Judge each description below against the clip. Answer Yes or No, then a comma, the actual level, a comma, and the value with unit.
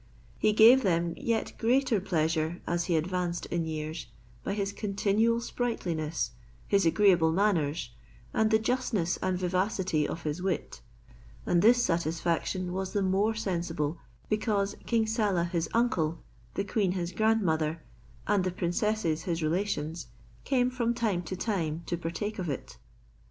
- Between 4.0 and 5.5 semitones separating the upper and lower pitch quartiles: Yes, average, 4.3 semitones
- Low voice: No, medium, 185 Hz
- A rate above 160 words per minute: No, average, 145 wpm